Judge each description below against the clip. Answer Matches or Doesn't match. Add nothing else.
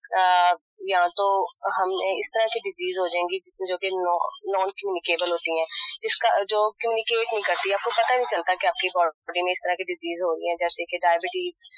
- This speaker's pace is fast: Matches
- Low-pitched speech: Doesn't match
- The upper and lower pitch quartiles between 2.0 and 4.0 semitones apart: Matches